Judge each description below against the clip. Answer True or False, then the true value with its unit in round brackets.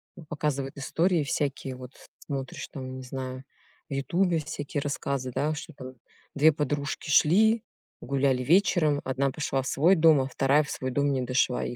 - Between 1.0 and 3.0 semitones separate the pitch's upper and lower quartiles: True (2.6 semitones)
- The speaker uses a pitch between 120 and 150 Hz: True (140 Hz)